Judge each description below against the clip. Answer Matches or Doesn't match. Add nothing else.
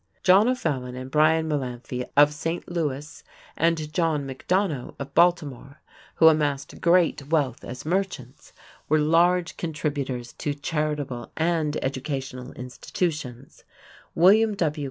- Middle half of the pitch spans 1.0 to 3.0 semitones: Doesn't match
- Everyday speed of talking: Doesn't match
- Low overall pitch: Doesn't match